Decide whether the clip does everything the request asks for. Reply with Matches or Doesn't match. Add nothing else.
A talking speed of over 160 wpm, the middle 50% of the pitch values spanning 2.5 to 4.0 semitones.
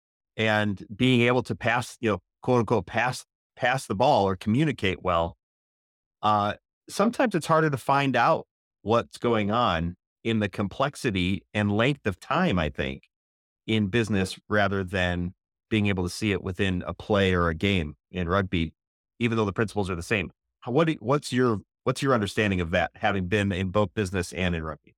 Doesn't match